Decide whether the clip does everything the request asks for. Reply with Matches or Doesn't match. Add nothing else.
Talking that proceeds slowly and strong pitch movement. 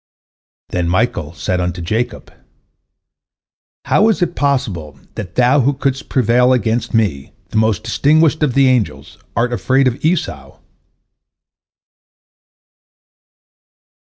Matches